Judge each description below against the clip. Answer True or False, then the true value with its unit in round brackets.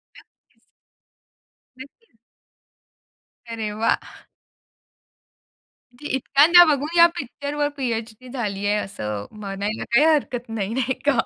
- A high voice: True (245 Hz)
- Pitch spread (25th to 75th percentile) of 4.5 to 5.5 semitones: True (5.2 semitones)